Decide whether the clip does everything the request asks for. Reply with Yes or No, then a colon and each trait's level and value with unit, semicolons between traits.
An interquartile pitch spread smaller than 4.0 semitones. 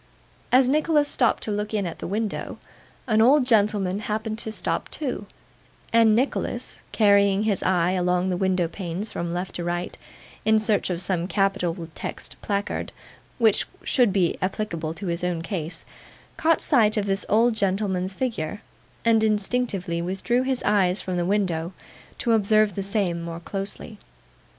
Yes: average, 3.4 semitones